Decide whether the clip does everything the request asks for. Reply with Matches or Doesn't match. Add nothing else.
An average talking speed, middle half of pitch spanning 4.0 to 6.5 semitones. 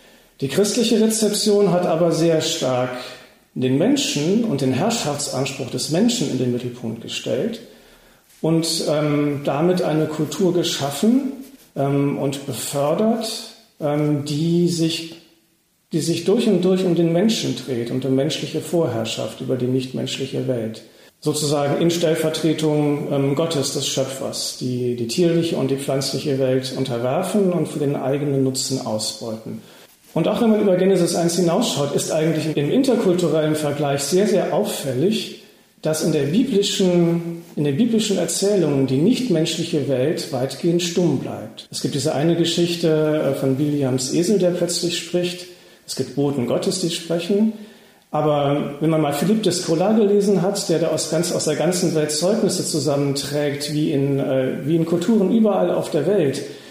Matches